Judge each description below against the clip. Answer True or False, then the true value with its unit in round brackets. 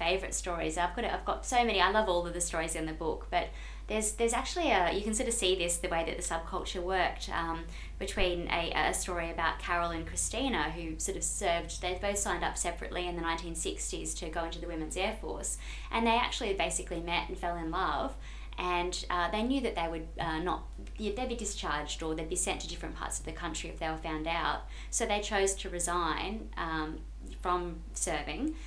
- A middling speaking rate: False (220 wpm)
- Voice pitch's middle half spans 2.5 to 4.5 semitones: True (2.9 semitones)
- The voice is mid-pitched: True (175 Hz)